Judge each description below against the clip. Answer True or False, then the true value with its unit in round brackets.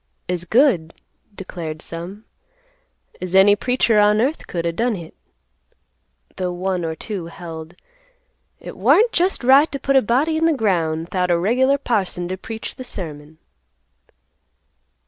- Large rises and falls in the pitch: True (6.5 semitones)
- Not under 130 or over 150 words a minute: True (145 wpm)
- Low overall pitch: False (190 Hz)